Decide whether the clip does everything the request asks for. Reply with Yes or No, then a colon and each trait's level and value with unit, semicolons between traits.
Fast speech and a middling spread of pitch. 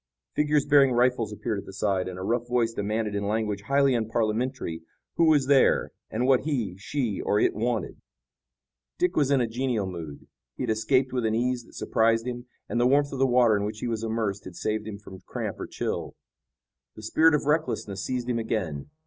Yes: fast, 210 wpm; average, 3.6 semitones